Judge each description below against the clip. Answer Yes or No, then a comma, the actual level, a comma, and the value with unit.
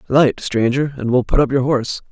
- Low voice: Yes, low, 130 Hz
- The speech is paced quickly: Yes, fast, 225 wpm